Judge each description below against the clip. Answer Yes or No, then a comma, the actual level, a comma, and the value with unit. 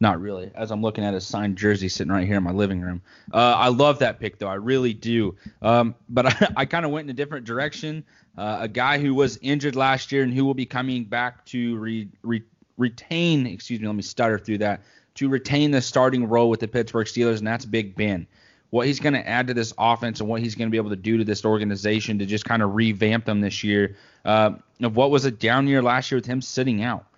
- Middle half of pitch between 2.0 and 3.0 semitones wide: No, average, 3.4 semitones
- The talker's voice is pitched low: Yes, low, 115 Hz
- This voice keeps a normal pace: No, fast, 255 wpm